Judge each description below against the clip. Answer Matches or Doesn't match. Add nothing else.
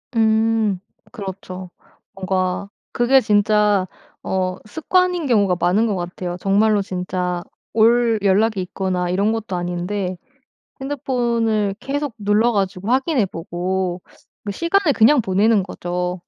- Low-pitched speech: Doesn't match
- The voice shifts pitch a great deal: Doesn't match